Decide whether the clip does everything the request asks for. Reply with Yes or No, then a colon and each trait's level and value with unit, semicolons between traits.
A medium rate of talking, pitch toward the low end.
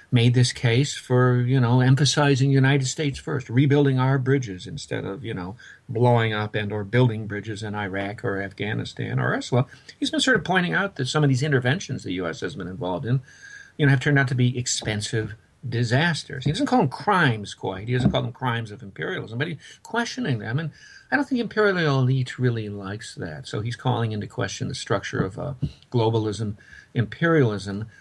Yes: average, 195 wpm; low, 130 Hz